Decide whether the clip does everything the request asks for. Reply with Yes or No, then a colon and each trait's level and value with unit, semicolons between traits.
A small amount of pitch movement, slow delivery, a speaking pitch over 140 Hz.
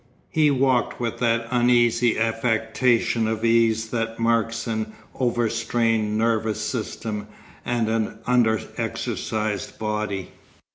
No: narrow, 1.4 semitones; slow, 105 wpm; low, 115 Hz